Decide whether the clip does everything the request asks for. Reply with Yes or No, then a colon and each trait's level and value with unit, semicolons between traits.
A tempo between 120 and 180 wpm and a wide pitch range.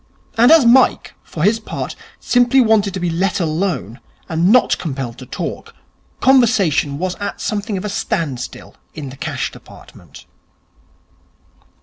Yes: average, 140 wpm; wide, 6.1 semitones